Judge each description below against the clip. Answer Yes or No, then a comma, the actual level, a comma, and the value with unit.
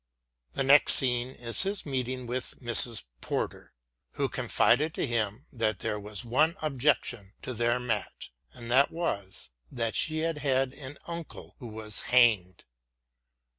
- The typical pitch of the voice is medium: No, low, 125 Hz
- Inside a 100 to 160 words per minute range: Yes, average, 145 wpm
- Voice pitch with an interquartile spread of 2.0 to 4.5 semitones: Yes, average, 3.7 semitones